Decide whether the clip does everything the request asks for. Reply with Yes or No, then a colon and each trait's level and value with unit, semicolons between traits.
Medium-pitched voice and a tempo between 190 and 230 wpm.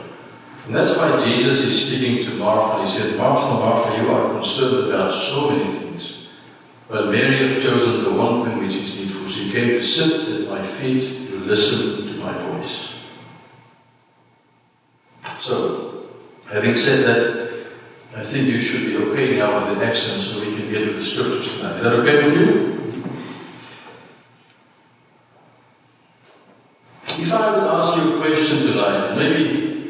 No: medium, 150 Hz; average, 155 wpm